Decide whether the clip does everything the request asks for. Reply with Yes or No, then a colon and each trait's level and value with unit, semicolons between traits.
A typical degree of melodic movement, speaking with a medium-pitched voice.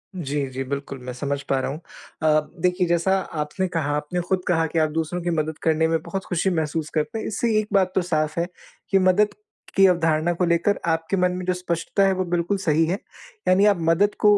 Yes: average, 3.2 semitones; medium, 170 Hz